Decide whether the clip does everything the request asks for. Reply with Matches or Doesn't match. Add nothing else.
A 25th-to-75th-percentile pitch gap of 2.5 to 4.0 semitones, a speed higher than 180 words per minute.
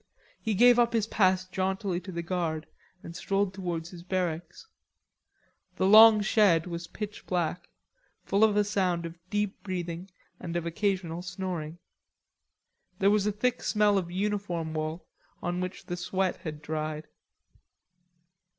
Doesn't match